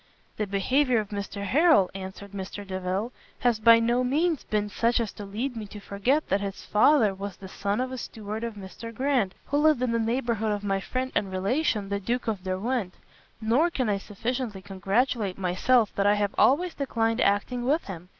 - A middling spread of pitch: Yes, average, 4.1 semitones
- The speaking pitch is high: Yes, high, 215 Hz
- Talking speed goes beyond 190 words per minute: Yes, average, 200 wpm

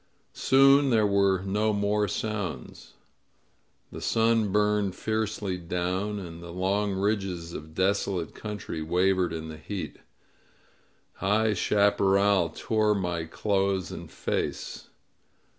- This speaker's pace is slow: Yes, slow, 110 wpm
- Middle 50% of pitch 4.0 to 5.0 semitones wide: No, narrow, 2.6 semitones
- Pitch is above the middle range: No, low, 100 Hz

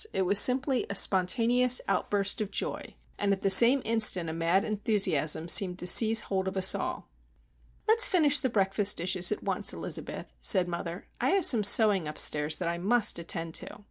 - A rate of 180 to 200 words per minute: Yes, average, 185 wpm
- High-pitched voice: Yes, high, 195 Hz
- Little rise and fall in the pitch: No, average, 4.4 semitones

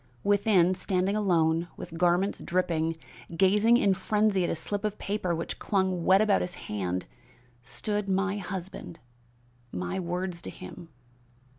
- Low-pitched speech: No, medium, 185 Hz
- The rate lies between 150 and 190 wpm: No, average, 140 wpm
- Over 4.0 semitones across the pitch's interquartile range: No, average, 3.0 semitones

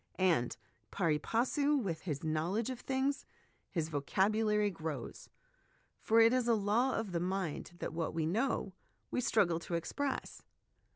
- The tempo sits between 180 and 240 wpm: No, average, 155 wpm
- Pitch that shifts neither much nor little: No, wide, 6.0 semitones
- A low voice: No, high, 195 Hz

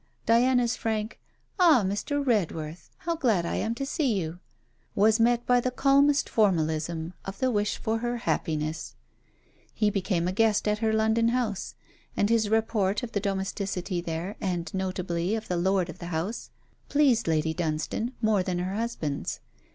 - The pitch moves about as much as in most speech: Yes, average, 4.7 semitones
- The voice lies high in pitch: Yes, high, 205 Hz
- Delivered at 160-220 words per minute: Yes, average, 165 wpm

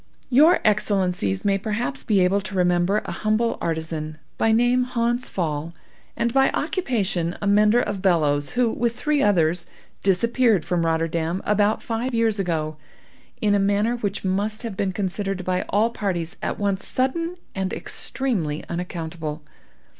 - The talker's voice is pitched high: Yes, high, 200 Hz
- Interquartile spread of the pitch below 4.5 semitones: No, average, 4.8 semitones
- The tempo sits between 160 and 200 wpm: No, average, 150 wpm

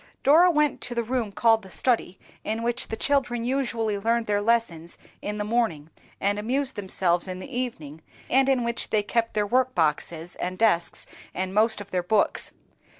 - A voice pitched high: Yes, high, 220 Hz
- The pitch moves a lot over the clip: No, average, 4.3 semitones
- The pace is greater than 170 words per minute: Yes, average, 180 wpm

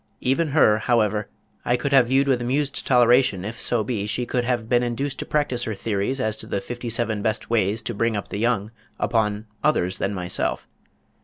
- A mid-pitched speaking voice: No, low, 115 Hz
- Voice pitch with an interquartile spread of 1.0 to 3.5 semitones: Yes, average, 3.1 semitones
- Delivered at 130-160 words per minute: No, fast, 205 wpm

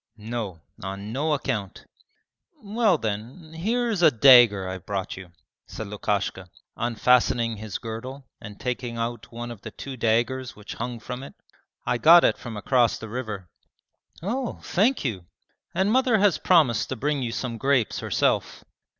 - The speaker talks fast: No, average, 160 wpm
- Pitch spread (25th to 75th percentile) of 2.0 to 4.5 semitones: No, wide, 5.5 semitones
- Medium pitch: No, low, 120 Hz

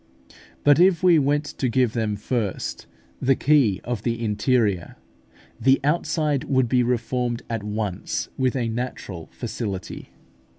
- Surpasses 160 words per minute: No, slow, 135 wpm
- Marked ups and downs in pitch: No, average, 3.8 semitones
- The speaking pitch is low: Yes, low, 125 Hz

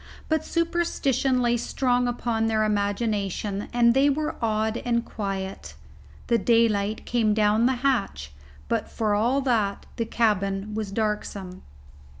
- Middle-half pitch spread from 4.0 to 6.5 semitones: No, average, 3.0 semitones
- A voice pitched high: Yes, high, 225 Hz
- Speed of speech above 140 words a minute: No, slow, 135 wpm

